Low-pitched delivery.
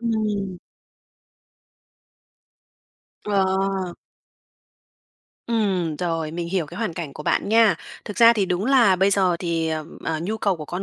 No: high, 190 Hz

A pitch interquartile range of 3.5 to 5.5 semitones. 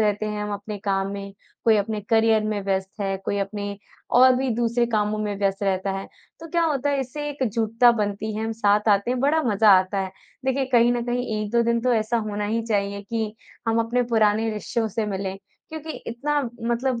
No: average, 2.9 semitones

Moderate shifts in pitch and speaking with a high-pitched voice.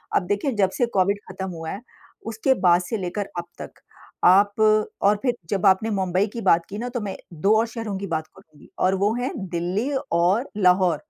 Yes: average, 3.3 semitones; high, 195 Hz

